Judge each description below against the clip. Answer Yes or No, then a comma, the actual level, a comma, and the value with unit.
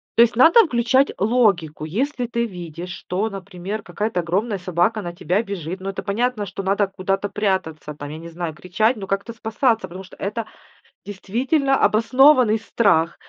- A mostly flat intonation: No, average, 4.3 semitones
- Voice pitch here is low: No, high, 200 Hz